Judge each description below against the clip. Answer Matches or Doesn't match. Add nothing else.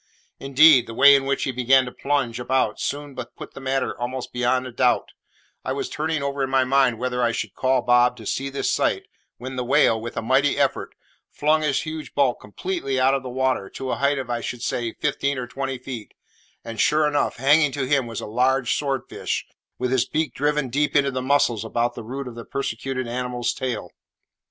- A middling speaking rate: Doesn't match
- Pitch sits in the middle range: Doesn't match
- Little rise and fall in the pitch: Matches